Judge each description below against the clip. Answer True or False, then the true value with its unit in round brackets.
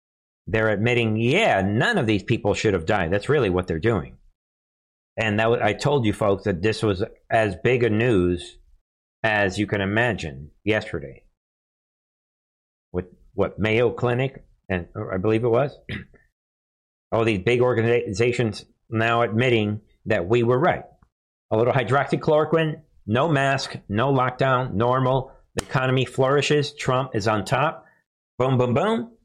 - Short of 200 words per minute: True (145 wpm)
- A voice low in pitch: True (115 Hz)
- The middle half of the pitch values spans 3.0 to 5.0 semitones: True (3.9 semitones)